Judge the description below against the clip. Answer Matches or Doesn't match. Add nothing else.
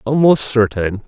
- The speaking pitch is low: Matches